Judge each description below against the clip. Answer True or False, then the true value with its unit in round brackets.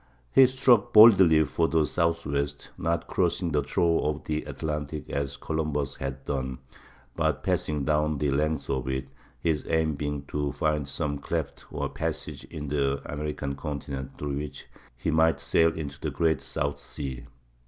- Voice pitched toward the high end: False (75 Hz)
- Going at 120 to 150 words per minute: False (160 wpm)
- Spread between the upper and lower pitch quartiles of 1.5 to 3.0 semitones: True (2.4 semitones)